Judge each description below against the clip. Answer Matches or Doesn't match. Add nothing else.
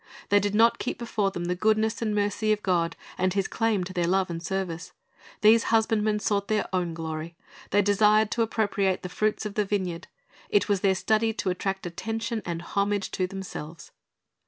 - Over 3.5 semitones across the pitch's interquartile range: Doesn't match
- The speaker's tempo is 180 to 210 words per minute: Matches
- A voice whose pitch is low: Doesn't match